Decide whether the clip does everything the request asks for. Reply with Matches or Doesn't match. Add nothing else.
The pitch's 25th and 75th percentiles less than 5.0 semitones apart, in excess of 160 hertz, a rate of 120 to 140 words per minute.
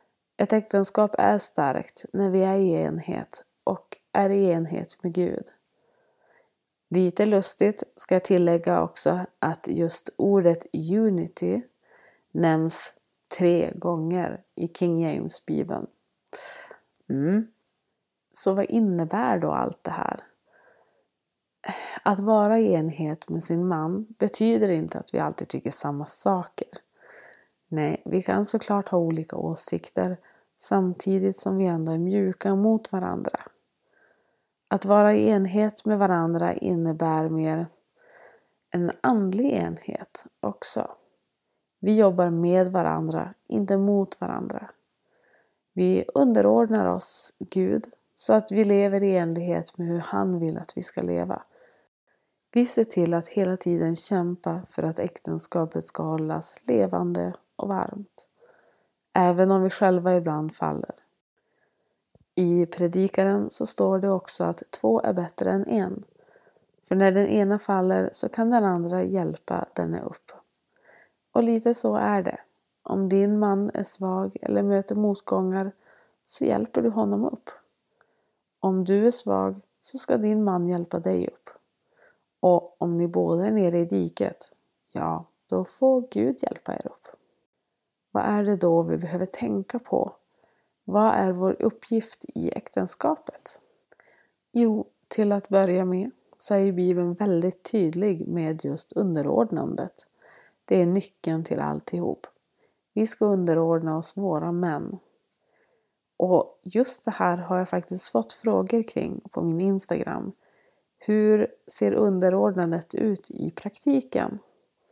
Matches